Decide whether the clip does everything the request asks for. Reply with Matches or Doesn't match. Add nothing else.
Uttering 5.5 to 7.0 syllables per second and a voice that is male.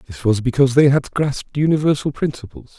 Matches